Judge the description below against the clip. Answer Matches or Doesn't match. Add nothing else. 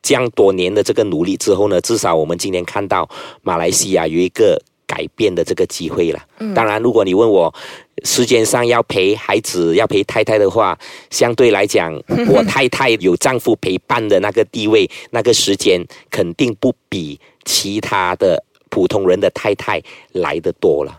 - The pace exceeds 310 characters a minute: Doesn't match